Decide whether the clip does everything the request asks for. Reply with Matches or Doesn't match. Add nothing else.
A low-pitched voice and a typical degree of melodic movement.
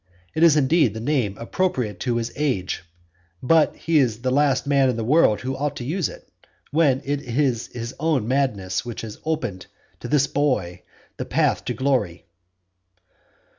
Matches